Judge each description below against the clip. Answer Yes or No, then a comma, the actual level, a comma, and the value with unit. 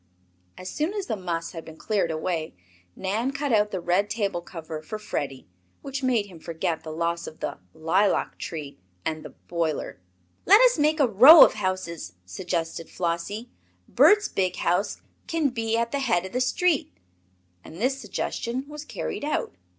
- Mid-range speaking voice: No, high, 195 Hz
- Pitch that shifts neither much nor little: No, wide, 7.4 semitones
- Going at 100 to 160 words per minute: No, average, 175 wpm